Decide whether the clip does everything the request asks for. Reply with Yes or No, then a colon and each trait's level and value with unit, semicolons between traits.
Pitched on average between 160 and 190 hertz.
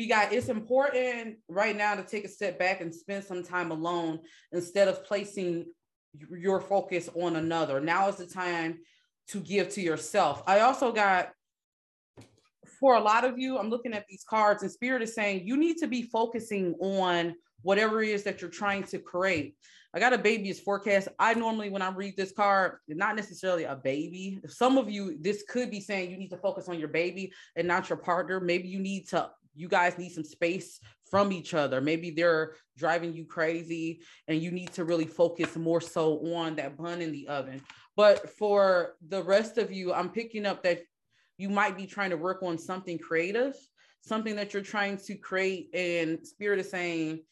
Yes: medium, 185 Hz